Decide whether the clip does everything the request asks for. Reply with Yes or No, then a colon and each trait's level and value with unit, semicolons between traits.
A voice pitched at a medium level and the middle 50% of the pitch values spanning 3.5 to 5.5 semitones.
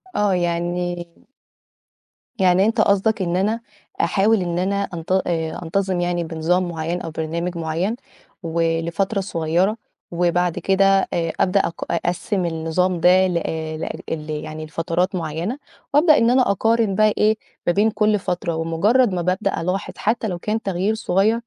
No: medium, 180 Hz; average, 3.1 semitones